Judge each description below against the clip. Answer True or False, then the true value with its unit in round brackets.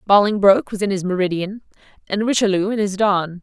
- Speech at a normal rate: True (175 wpm)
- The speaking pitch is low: False (200 Hz)